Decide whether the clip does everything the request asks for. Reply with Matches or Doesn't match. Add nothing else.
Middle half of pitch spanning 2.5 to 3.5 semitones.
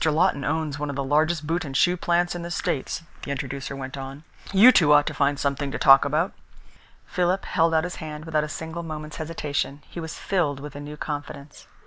Matches